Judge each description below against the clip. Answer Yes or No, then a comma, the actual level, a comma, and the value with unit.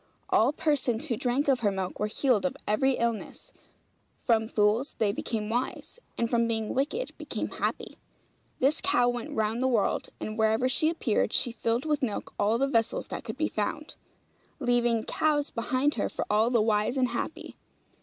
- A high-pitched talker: Yes, high, 235 Hz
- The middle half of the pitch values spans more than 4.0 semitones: No, average, 3.5 semitones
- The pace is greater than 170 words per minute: Yes, average, 180 wpm